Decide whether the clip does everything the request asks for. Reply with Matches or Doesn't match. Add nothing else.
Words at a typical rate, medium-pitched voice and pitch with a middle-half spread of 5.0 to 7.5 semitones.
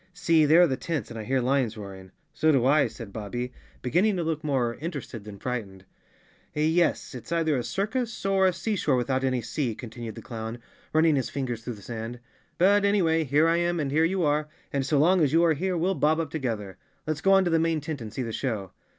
Doesn't match